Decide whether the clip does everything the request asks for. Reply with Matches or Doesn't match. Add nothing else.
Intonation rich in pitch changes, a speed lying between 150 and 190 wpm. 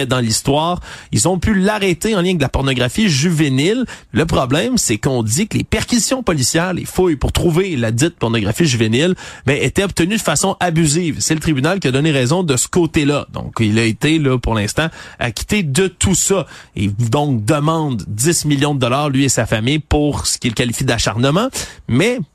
Doesn't match